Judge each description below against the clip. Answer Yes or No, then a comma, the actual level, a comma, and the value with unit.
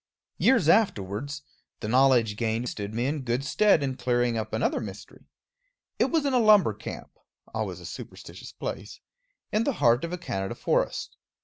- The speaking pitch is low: Yes, low, 125 Hz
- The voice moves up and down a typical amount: No, wide, 7.7 semitones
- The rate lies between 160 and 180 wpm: Yes, average, 170 wpm